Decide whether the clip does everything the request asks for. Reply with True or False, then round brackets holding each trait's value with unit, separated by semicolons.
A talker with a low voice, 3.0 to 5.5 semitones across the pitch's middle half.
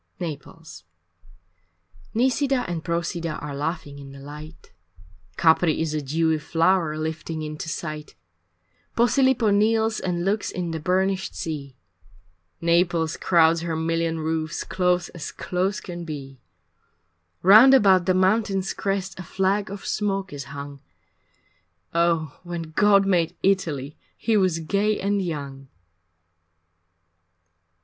False (170 Hz; 3.7 semitones)